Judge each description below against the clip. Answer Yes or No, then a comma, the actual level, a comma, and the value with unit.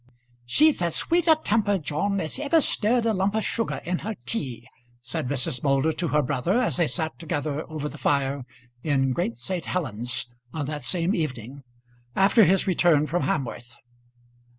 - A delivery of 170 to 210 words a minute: Yes, average, 175 wpm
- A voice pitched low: No, medium, 160 Hz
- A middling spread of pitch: No, wide, 6.3 semitones